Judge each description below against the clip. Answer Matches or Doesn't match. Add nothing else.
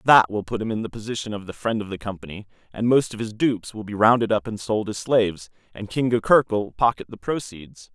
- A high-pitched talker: Doesn't match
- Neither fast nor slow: Doesn't match